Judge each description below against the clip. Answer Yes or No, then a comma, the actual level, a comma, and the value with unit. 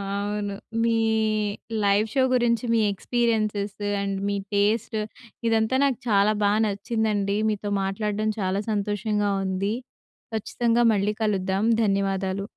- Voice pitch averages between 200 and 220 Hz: Yes, high, 205 Hz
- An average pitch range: No, narrow, 1.8 semitones